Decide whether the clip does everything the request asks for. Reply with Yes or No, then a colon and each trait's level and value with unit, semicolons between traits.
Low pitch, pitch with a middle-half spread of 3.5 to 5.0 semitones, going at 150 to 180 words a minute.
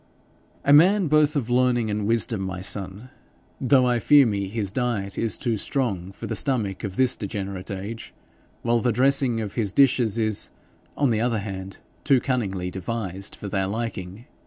Yes: low, 110 Hz; average, 4.3 semitones; average, 175 wpm